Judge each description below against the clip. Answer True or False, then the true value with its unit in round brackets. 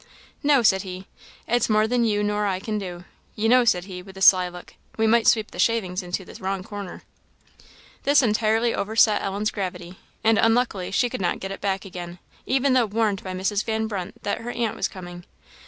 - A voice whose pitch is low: False (205 Hz)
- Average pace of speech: False (210 wpm)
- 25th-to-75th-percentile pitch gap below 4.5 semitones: True (3.3 semitones)